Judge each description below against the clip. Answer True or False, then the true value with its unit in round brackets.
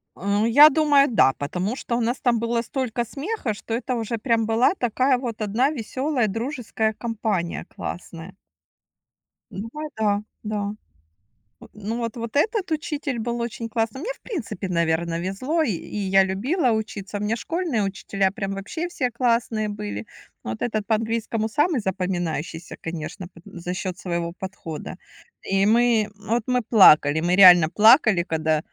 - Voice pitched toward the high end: True (220 Hz)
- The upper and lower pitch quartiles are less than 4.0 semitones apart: False (4.3 semitones)